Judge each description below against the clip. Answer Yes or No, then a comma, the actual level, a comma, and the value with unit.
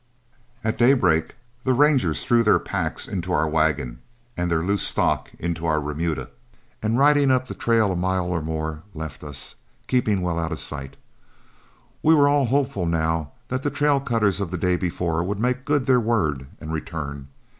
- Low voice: Yes, very low, 90 Hz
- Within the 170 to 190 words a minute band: Yes, average, 180 wpm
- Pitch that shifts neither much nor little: No, wide, 7.6 semitones